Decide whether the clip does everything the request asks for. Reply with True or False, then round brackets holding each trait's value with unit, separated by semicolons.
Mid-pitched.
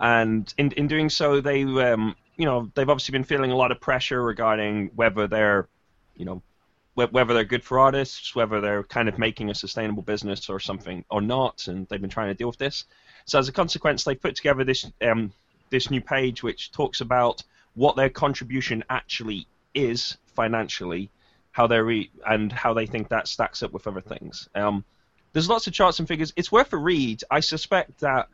False (120 Hz)